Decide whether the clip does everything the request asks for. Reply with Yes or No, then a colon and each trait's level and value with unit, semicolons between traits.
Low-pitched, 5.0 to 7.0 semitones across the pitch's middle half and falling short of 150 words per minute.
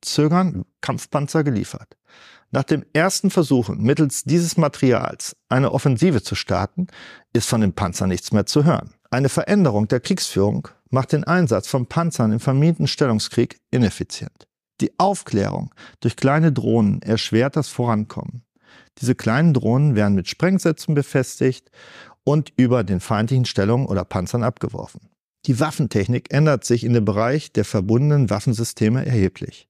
Yes: low, 130 Hz; average, 5.3 semitones; average, 140 wpm